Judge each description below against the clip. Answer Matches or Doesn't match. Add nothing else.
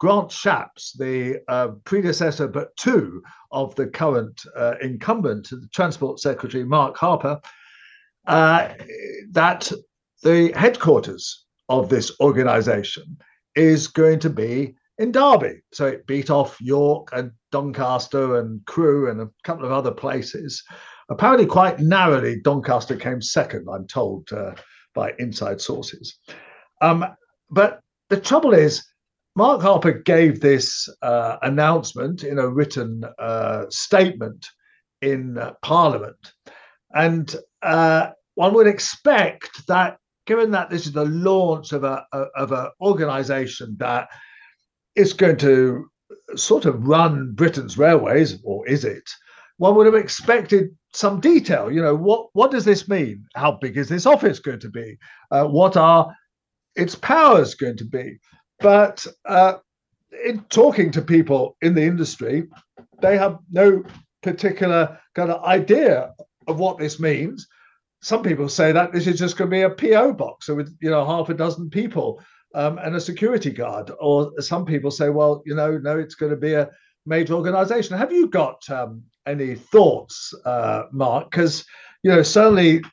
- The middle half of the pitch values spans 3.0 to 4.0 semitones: Doesn't match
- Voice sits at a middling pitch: Matches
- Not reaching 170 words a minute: Matches